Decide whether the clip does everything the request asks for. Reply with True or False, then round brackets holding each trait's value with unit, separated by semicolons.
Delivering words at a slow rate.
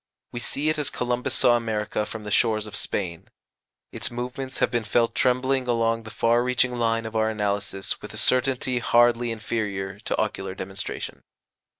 False (175 wpm)